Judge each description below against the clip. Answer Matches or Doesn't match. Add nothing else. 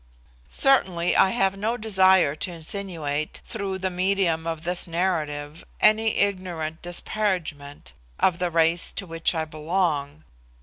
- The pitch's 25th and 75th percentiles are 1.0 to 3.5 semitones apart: Matches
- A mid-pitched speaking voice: Matches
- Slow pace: Matches